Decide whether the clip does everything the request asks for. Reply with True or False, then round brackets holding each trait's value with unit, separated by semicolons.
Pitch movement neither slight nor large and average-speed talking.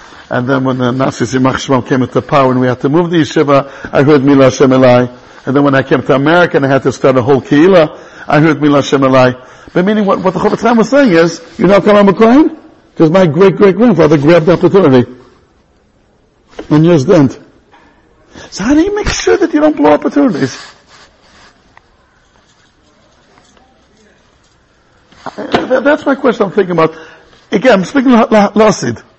False (7.4 semitones; 175 wpm)